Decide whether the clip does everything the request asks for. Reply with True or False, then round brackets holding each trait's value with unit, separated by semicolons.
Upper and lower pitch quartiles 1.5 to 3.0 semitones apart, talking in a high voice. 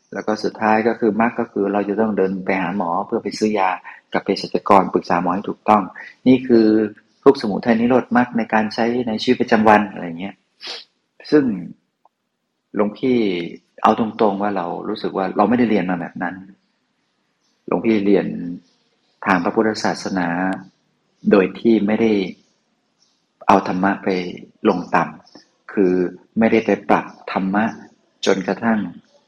False (2.7 semitones; 110 Hz)